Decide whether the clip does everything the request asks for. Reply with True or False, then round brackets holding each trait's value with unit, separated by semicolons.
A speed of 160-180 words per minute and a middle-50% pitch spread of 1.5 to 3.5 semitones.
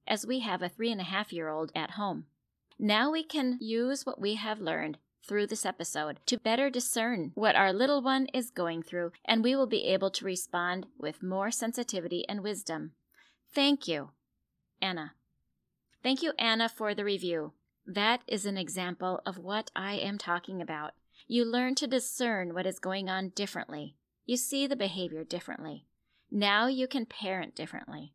False (175 wpm; 5.1 semitones)